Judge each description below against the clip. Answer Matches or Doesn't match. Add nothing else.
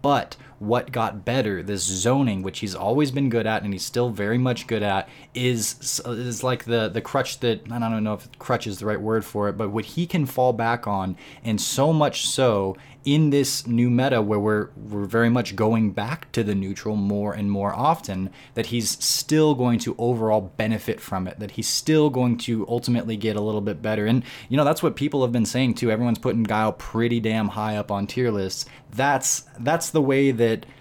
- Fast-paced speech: Matches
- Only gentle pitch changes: Doesn't match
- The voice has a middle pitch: Doesn't match